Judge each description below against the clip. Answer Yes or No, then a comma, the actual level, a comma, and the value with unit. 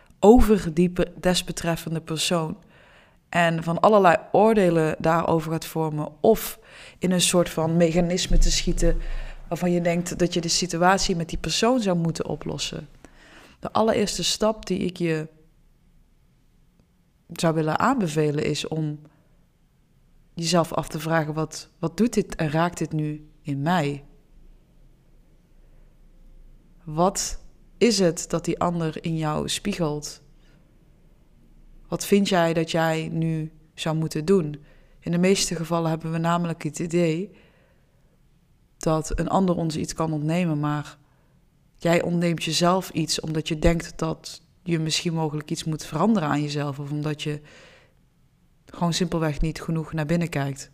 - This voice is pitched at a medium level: Yes, medium, 165 Hz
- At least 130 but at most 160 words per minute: Yes, average, 140 wpm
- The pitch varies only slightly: Yes, narrow, 1.9 semitones